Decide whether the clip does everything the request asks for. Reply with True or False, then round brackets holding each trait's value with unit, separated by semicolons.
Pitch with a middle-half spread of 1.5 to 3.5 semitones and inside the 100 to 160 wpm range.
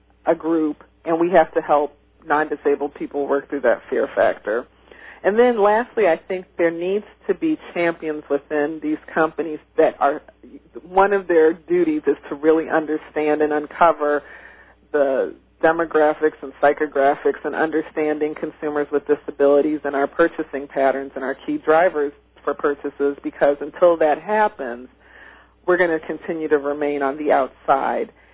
True (2.6 semitones; 150 wpm)